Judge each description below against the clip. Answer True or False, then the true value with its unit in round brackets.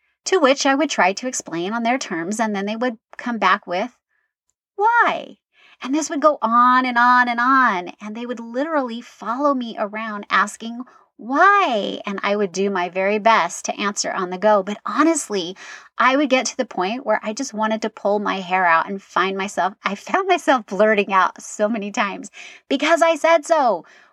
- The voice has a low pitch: False (230 Hz)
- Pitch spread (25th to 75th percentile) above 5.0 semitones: True (5.4 semitones)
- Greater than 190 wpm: True (200 wpm)